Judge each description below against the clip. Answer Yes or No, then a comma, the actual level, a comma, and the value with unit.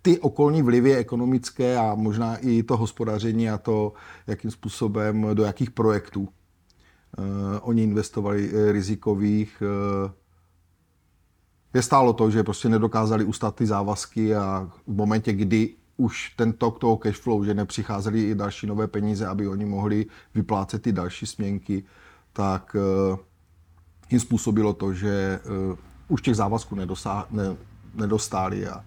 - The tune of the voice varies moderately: No, narrow, 2.3 semitones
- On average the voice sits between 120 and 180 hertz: No, low, 105 Hz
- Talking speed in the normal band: Yes, average, 135 wpm